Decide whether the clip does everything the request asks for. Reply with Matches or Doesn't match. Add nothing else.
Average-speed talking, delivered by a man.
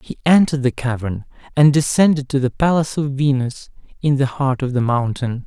Matches